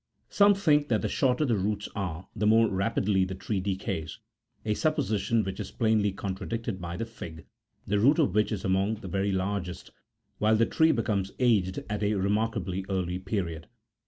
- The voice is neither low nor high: No, low, 105 Hz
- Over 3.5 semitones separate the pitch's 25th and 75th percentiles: No, average, 3.2 semitones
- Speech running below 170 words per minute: No, average, 185 wpm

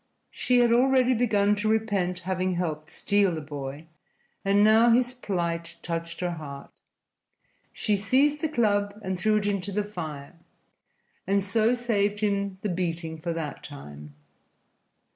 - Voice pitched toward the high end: Yes, high, 200 Hz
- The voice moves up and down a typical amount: Yes, average, 4.4 semitones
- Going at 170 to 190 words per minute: No, average, 145 wpm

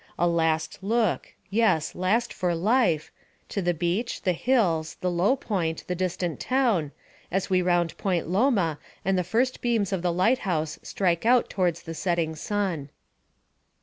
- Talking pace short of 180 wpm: Yes, average, 160 wpm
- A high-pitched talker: No, medium, 180 Hz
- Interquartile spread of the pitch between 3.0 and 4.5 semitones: Yes, average, 4.2 semitones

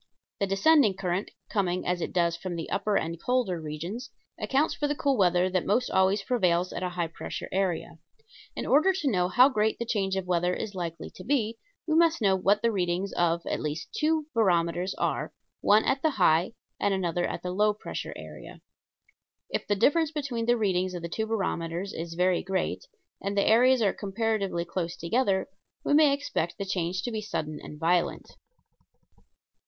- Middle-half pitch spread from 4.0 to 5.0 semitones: Yes, average, 4.7 semitones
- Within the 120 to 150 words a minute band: No, average, 190 wpm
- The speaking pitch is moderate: No, high, 195 Hz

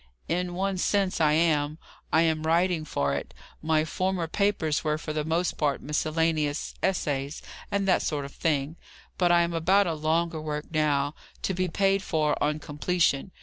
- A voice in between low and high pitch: Yes, medium, 160 Hz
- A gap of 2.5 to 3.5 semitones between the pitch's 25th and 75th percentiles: Yes, average, 2.9 semitones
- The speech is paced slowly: No, average, 175 wpm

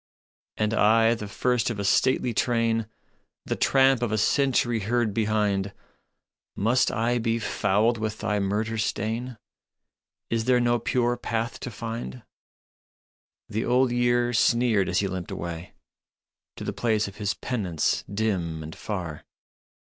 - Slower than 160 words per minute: Yes, average, 145 wpm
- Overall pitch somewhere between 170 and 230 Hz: No, low, 110 Hz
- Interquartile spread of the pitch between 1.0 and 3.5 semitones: Yes, average, 2.9 semitones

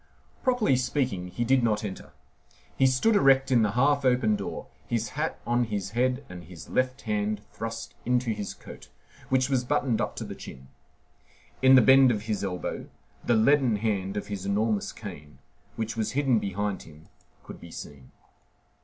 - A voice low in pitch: Yes, low, 115 Hz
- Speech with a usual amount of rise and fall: Yes, average, 4.3 semitones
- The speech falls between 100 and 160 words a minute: No, average, 175 wpm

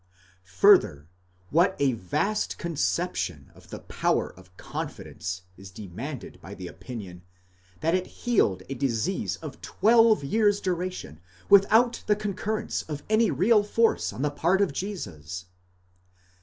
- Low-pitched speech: No, medium, 155 Hz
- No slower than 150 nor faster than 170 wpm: No, average, 140 wpm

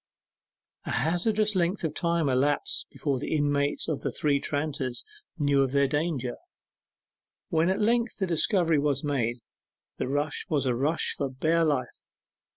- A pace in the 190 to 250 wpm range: No, average, 155 wpm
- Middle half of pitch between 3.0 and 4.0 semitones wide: Yes, average, 3.4 semitones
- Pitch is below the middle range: No, medium, 145 Hz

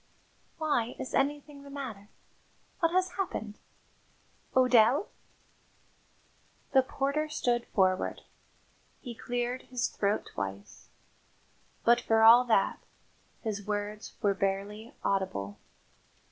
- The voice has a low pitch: No, high, 235 Hz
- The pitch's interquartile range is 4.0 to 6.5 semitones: Yes, average, 4.7 semitones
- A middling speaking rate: No, slow, 100 wpm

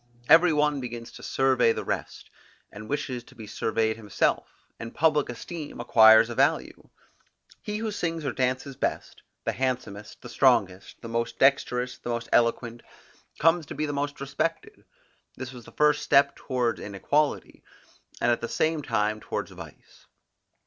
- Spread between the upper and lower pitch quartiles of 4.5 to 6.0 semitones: No, average, 4.1 semitones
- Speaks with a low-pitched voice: Yes, low, 130 Hz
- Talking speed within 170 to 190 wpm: No, average, 160 wpm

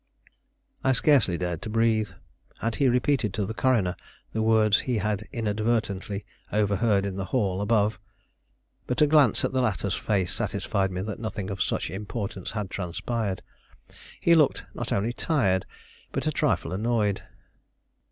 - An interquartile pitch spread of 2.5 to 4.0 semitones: Yes, average, 3.2 semitones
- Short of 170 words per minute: Yes, average, 150 wpm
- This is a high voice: No, low, 105 Hz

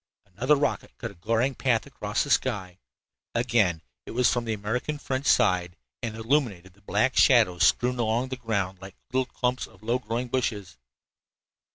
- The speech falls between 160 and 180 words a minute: Yes, average, 170 wpm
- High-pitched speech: No, low, 115 Hz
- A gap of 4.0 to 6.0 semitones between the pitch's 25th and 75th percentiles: Yes, average, 4.4 semitones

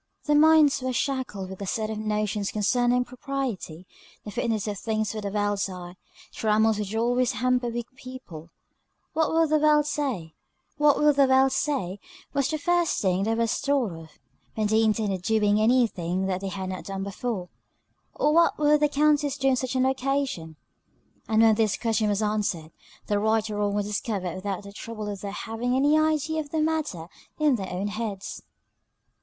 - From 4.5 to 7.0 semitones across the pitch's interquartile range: Yes, average, 5.2 semitones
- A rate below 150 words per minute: No, average, 175 wpm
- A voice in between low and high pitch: No, high, 225 Hz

